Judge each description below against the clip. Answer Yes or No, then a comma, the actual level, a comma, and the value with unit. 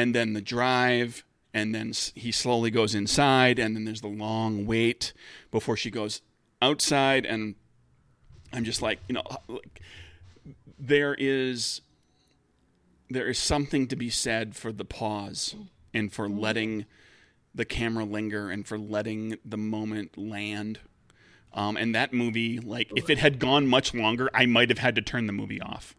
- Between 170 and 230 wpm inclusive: No, average, 160 wpm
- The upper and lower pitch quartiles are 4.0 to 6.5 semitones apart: No, average, 2.9 semitones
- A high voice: No, low, 110 Hz